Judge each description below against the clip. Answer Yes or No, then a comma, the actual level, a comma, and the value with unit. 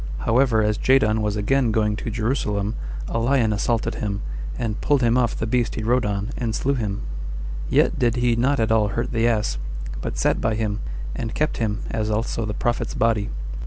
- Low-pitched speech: Yes, low, 115 Hz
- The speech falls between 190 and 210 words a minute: Yes, average, 200 wpm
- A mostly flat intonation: Yes, narrow, 2.2 semitones